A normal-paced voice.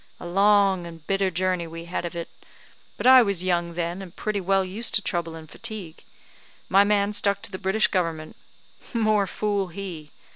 Yes: average, 185 wpm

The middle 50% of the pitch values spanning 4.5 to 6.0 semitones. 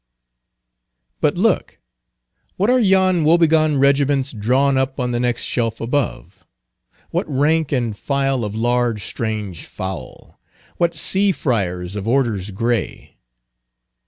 Yes: average, 5.1 semitones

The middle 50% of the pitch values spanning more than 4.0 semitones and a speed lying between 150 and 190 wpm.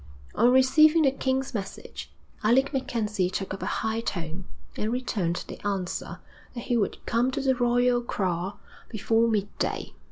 Yes: average, 4.5 semitones; average, 155 wpm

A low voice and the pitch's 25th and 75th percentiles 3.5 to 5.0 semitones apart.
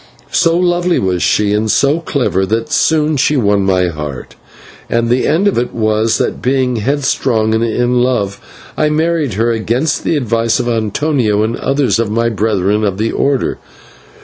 Yes: low, 115 Hz; average, 4.7 semitones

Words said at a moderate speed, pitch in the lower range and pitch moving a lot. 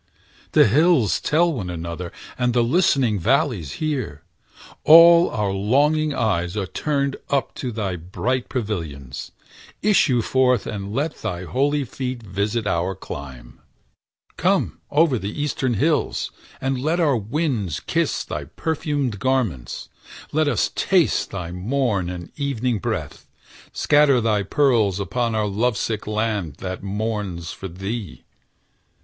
No: slow, 130 wpm; low, 115 Hz; wide, 6.3 semitones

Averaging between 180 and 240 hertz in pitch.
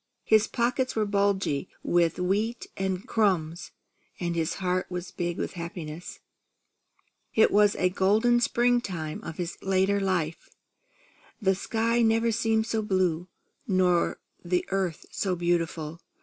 Yes: high, 190 Hz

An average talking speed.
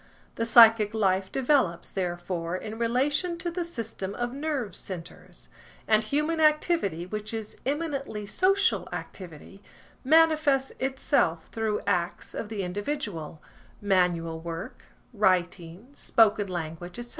No: slow, 115 wpm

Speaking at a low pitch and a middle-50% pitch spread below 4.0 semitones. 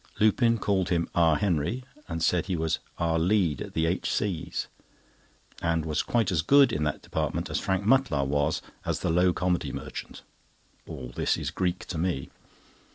Yes: very low, 85 Hz; average, 3.3 semitones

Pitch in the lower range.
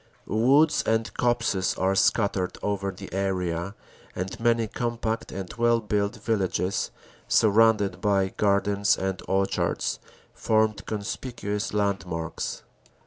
Yes: low, 100 Hz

